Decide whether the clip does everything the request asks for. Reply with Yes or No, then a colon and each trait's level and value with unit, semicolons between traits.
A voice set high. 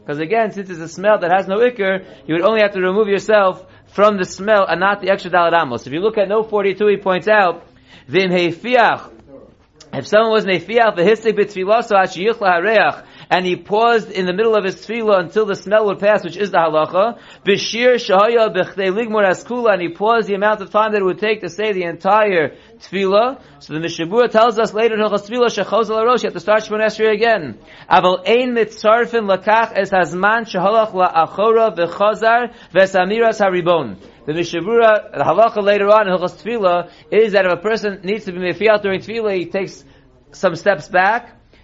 Yes: high, 200 Hz